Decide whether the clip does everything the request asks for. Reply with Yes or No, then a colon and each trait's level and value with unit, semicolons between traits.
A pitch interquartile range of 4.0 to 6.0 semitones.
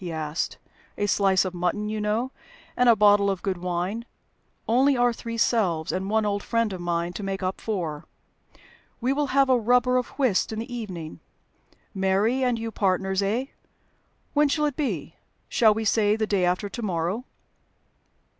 Yes: average, 4.3 semitones